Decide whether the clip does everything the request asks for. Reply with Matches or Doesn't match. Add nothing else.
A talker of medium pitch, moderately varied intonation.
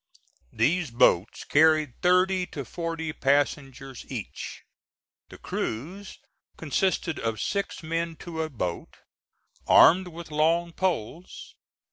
Matches